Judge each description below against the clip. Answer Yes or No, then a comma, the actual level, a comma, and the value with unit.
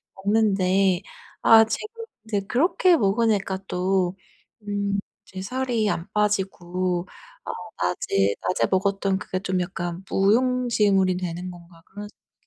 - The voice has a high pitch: Yes, high, 195 Hz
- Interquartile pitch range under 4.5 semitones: Yes, average, 2.9 semitones